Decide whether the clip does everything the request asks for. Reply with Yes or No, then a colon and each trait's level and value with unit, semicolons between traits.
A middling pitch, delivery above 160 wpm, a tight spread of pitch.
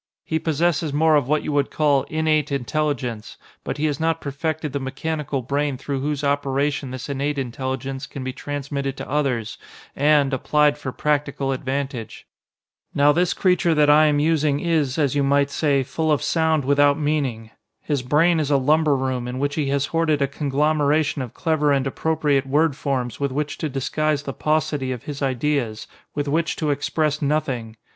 Yes: medium, 145 Hz; average, 180 wpm; narrow, 2.1 semitones